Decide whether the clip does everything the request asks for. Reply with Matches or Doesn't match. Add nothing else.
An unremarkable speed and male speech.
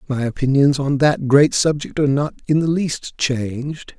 Matches